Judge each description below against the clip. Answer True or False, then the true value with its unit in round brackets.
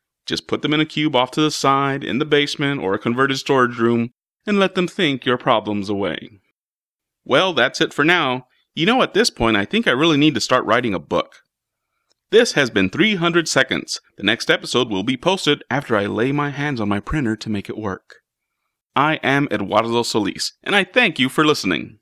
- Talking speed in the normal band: False (215 wpm)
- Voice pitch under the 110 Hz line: False (140 Hz)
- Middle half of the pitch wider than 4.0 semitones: True (4.9 semitones)